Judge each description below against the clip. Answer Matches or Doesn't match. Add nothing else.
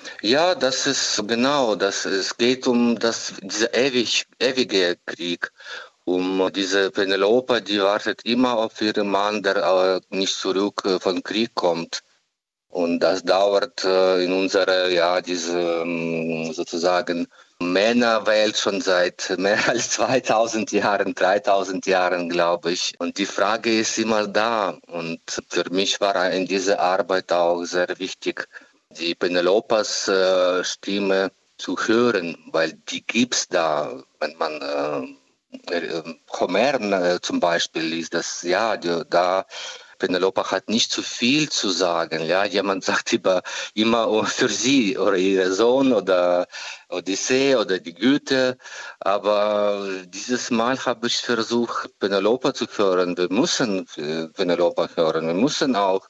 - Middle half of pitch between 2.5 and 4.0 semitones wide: Matches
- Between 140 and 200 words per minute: Doesn't match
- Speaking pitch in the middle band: Doesn't match